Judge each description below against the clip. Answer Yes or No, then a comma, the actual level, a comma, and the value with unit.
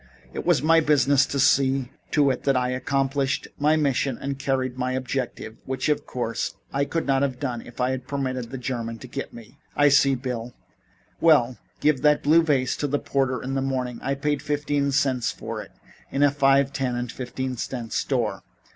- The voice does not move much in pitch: Yes, narrow, 1.9 semitones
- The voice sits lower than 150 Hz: Yes, low, 135 Hz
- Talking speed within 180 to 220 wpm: Yes, average, 200 wpm